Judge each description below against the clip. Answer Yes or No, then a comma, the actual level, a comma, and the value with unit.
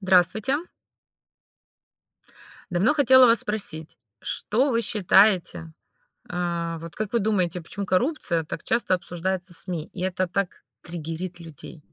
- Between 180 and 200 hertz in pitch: Yes, medium, 185 Hz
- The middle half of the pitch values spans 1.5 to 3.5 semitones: No, average, 4.1 semitones